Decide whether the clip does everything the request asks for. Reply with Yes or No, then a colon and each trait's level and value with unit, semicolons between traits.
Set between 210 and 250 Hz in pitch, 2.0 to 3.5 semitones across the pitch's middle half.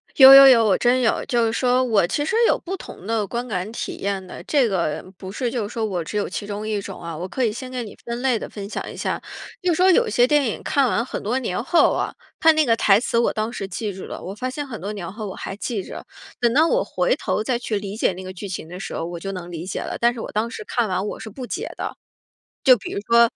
No: high, 225 Hz; average, 4.5 semitones